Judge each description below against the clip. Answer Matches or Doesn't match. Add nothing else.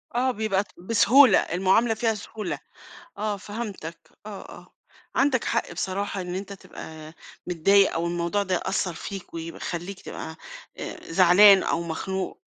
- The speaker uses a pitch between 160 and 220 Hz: Matches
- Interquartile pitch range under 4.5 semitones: Matches